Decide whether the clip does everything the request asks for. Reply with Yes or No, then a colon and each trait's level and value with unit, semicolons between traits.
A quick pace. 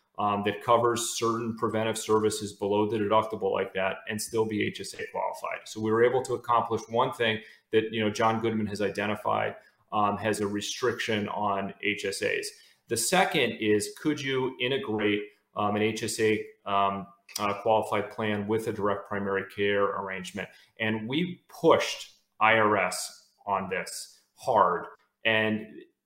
No: average, 145 wpm